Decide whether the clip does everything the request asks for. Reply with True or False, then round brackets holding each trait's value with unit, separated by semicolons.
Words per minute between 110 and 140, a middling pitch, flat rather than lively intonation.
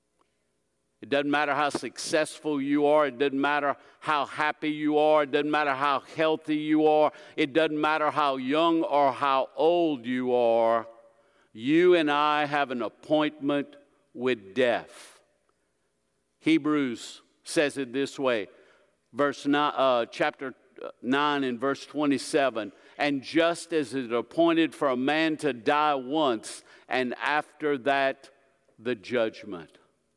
True (135 wpm; 145 Hz; 2.1 semitones)